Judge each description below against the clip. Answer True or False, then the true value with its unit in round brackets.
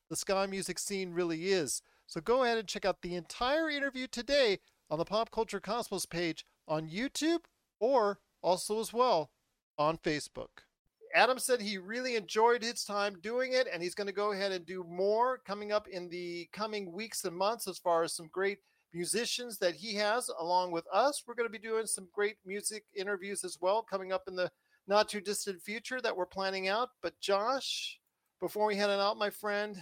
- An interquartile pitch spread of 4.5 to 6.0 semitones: False (3.8 semitones)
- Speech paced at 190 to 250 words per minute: True (200 wpm)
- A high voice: True (205 Hz)